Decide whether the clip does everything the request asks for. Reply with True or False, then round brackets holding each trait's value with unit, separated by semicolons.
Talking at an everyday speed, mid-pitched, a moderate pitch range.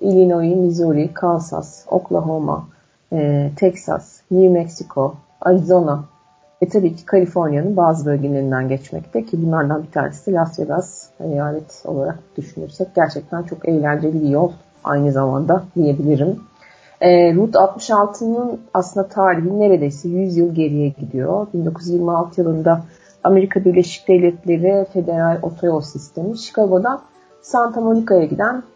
True (115 wpm; 170 Hz; 3.9 semitones)